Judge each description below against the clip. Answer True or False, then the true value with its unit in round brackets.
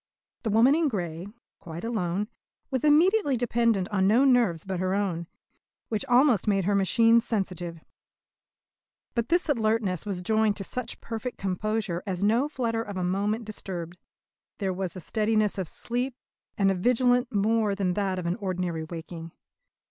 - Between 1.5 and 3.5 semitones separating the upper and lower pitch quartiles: False (4.2 semitones)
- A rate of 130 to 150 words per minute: False (160 wpm)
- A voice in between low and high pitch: False (205 Hz)